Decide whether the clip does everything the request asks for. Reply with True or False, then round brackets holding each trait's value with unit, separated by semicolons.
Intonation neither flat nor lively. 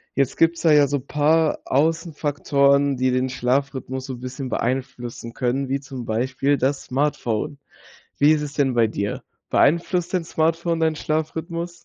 True (3.3 semitones)